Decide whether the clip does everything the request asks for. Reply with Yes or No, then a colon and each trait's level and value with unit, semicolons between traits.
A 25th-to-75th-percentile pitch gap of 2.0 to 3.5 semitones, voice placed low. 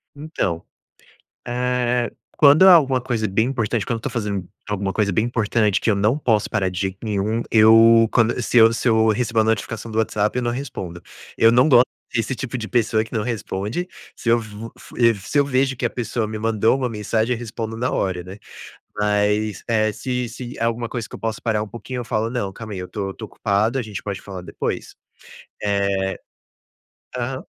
Yes: average, 2.7 semitones; low, 115 Hz